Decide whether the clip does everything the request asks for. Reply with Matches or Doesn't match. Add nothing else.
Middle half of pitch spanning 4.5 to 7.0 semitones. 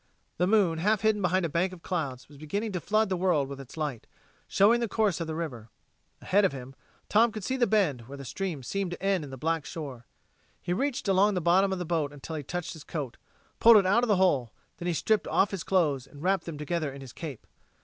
Matches